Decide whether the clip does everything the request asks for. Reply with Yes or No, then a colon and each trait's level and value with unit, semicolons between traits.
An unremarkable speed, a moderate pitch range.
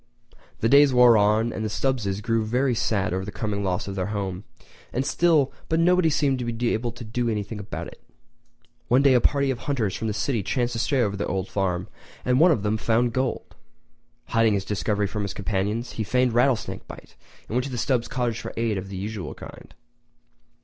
No: fast, 210 wpm; average, 3.6 semitones